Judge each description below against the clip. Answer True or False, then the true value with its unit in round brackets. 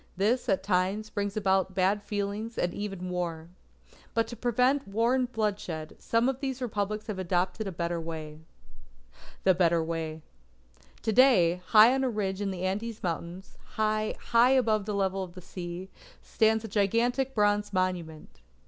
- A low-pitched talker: False (200 Hz)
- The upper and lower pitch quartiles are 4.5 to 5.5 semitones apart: False (3.7 semitones)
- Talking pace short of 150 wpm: False (165 wpm)